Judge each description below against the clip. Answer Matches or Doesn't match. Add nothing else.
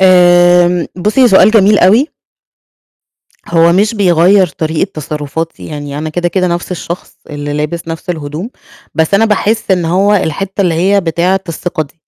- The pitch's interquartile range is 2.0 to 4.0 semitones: Matches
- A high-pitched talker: Doesn't match